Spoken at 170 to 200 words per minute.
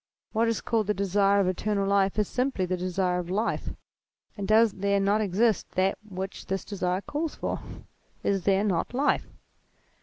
Yes: average, 175 wpm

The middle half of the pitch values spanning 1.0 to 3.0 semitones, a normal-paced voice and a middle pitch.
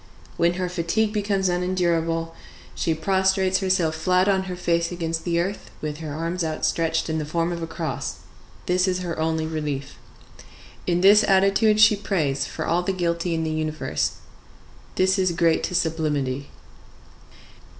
Yes: average, 2.7 semitones; average, 160 wpm; medium, 170 Hz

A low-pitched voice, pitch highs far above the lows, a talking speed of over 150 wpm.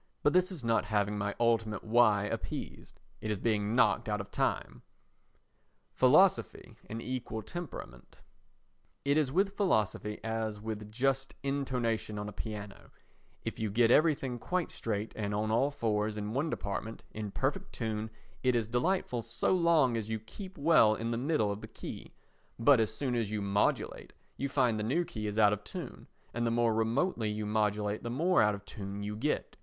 No: low, 115 Hz; average, 4.1 semitones; average, 180 wpm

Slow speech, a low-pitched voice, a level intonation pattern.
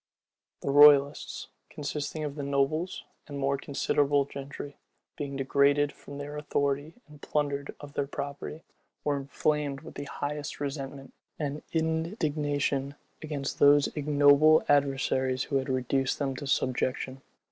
No: slow, 130 wpm; medium, 145 Hz; narrow, 1.1 semitones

